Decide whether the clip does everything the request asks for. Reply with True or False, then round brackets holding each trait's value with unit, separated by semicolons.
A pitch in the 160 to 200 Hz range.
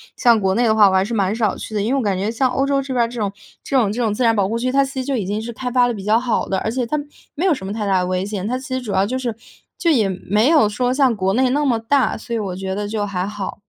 False (225 Hz)